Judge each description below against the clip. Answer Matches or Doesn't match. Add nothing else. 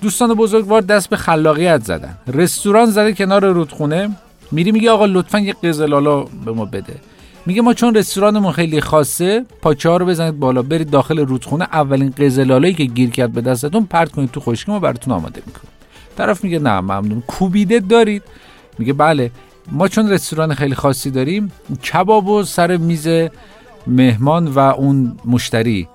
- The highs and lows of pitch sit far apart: Matches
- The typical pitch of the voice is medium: Matches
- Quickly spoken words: Matches